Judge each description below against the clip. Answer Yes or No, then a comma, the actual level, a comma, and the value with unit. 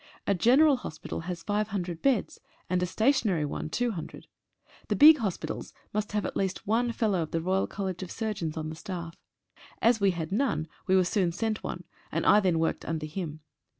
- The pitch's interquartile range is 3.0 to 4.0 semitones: No, average, 4.7 semitones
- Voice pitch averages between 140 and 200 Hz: Yes, high, 190 Hz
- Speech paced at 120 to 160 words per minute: No, average, 175 wpm